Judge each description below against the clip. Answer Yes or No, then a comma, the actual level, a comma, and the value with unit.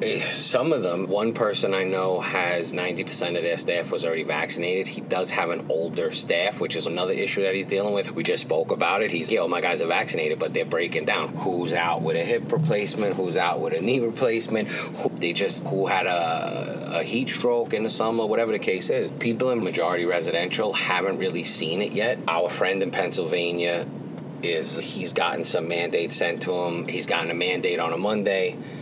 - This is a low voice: Yes, low, 115 Hz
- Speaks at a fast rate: Yes, fast, 215 wpm